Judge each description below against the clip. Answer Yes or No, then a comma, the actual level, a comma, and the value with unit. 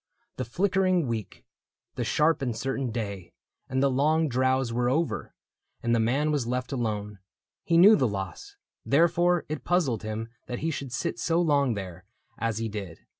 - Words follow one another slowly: No, average, 175 wpm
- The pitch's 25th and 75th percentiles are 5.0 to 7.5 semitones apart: Yes, wide, 5.4 semitones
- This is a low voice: Yes, low, 130 Hz